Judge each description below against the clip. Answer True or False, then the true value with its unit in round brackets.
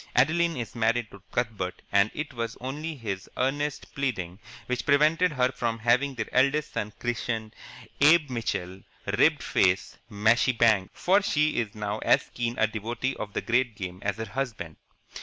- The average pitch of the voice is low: True (120 Hz)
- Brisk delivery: False (165 wpm)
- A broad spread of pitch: False (4.4 semitones)